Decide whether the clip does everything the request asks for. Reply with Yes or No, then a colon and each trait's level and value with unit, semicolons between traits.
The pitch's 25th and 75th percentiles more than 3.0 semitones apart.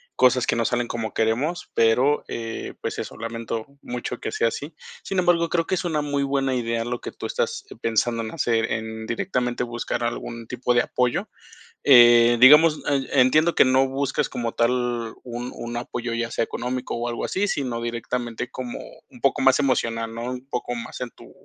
No: average, 2.7 semitones